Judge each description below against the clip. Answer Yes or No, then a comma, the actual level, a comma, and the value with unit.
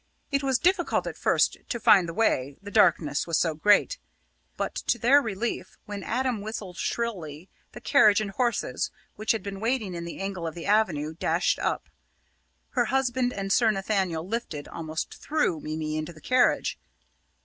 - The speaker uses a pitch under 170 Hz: No, high, 205 Hz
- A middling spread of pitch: No, wide, 6.1 semitones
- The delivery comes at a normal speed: Yes, average, 170 wpm